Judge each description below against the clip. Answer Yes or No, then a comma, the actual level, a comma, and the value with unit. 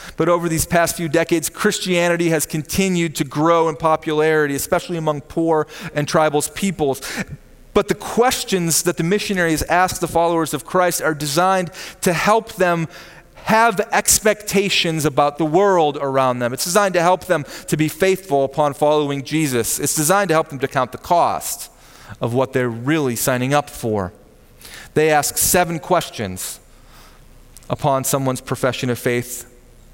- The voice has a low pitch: No, medium, 155 Hz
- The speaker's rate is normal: Yes, average, 155 wpm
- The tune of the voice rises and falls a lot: No, average, 4.4 semitones